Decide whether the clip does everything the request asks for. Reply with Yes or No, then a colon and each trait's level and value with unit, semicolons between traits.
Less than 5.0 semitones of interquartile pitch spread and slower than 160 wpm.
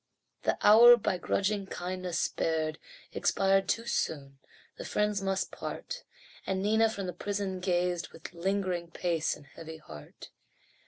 Yes: average, 3.1 semitones; average, 140 wpm